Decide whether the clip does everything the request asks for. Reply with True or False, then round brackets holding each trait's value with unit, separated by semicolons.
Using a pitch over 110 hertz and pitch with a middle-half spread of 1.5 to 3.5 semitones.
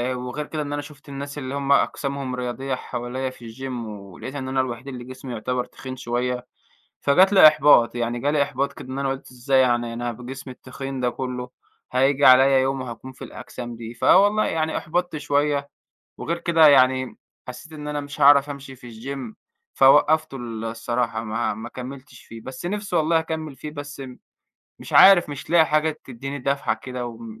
True (135 Hz; 2.8 semitones)